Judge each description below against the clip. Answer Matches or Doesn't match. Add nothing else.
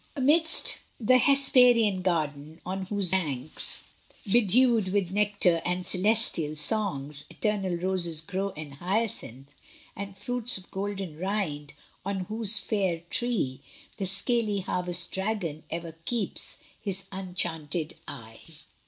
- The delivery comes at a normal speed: Doesn't match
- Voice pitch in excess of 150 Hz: Matches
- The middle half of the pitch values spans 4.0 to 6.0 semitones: Matches